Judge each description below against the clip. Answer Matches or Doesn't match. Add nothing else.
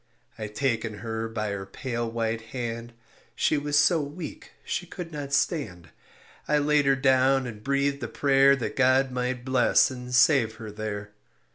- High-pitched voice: Doesn't match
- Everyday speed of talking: Matches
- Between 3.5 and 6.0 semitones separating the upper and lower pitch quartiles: Matches